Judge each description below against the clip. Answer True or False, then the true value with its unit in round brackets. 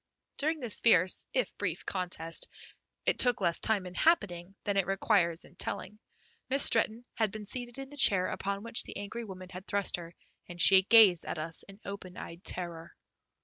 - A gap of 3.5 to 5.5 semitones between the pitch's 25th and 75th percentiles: True (4.2 semitones)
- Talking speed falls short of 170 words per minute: False (190 wpm)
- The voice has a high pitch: True (195 Hz)